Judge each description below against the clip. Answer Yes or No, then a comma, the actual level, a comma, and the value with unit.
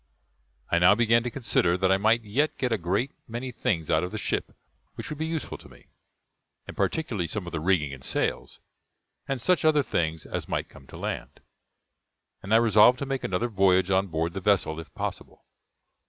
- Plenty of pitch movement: Yes, wide, 5.7 semitones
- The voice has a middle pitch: No, low, 100 Hz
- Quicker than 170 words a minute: Yes, average, 200 wpm